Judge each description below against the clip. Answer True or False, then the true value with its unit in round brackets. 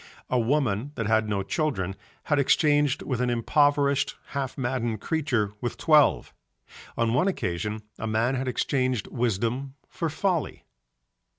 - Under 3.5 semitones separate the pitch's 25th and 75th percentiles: False (4.4 semitones)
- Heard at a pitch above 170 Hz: False (125 Hz)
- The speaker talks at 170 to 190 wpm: False (135 wpm)